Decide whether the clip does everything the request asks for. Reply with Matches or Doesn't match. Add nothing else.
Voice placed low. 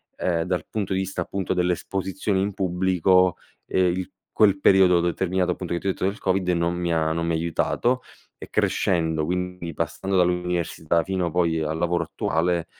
Matches